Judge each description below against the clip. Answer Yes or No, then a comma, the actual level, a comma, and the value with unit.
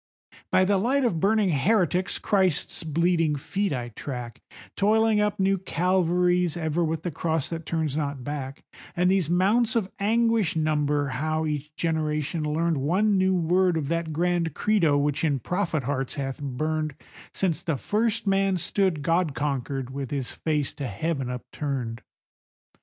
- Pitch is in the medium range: Yes, medium, 165 Hz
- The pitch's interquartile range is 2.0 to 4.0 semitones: No, average, 4.5 semitones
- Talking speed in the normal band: Yes, average, 155 wpm